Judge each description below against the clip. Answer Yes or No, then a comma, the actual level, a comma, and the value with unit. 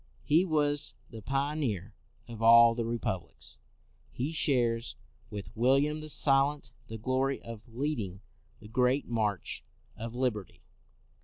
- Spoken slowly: Yes, slow, 130 wpm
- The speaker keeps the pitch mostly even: No, average, 3.8 semitones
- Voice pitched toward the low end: Yes, low, 120 Hz